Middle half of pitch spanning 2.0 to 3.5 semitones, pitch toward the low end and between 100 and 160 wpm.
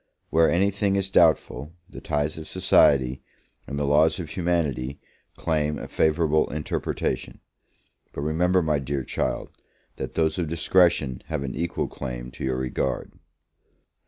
Yes: average, 3.2 semitones; very low, 75 Hz; average, 145 wpm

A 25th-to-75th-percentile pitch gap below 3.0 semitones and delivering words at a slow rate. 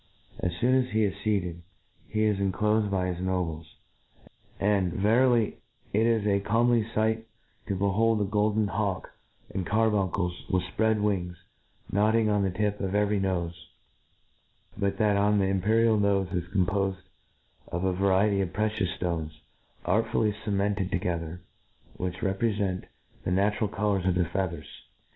No: narrow, 2.5 semitones; average, 155 wpm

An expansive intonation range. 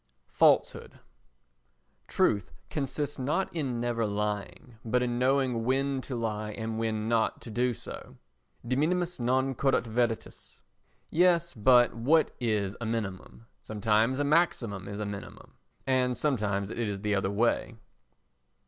No: average, 3.8 semitones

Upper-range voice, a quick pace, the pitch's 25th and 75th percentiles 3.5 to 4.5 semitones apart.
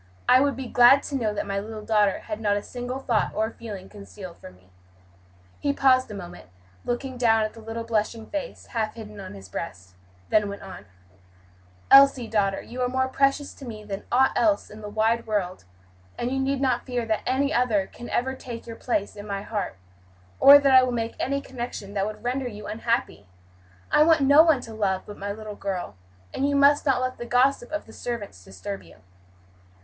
Yes: high, 230 Hz; fast, 210 wpm; average, 4.1 semitones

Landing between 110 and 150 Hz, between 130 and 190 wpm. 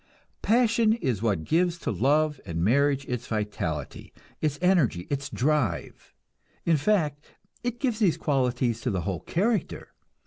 Yes: medium, 140 Hz; average, 140 wpm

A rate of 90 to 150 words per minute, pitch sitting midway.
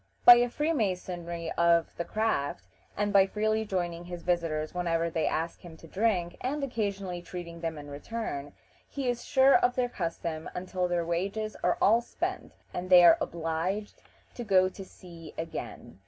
No: average, 170 wpm; medium, 180 Hz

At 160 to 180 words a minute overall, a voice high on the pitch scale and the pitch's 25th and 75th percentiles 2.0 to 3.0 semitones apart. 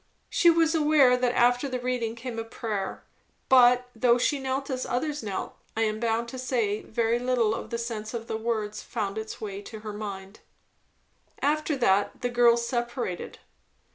Yes: average, 175 wpm; high, 235 Hz; narrow, 2.5 semitones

